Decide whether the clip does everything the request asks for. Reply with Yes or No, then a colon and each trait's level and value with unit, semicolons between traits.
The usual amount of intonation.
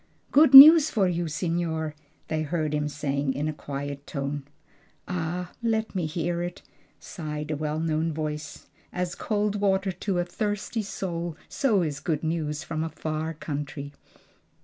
Yes: average, 3.3 semitones